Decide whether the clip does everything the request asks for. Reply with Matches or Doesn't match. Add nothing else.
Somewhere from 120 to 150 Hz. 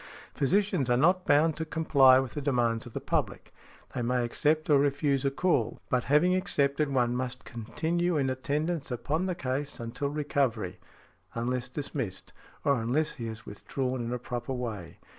Matches